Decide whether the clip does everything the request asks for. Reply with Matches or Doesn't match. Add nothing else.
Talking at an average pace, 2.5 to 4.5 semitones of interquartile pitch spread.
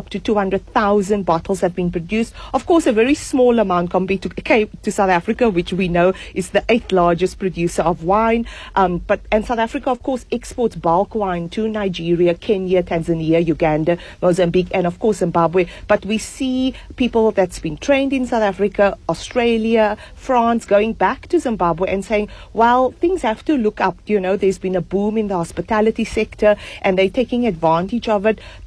Matches